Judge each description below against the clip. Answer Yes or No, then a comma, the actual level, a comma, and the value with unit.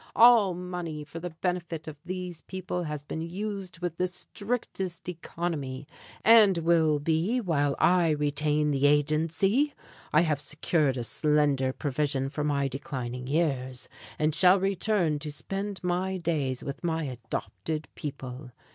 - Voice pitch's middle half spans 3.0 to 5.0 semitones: Yes, average, 3.7 semitones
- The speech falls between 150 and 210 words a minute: No, average, 140 wpm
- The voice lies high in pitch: No, medium, 160 Hz